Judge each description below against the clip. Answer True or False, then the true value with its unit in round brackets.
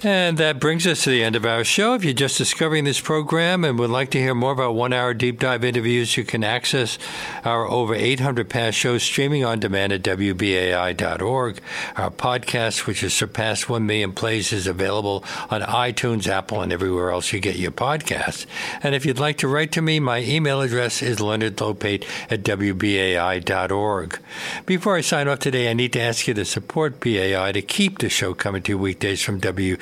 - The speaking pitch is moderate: False (115 Hz)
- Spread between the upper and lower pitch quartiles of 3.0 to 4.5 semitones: False (5.2 semitones)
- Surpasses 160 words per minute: True (195 wpm)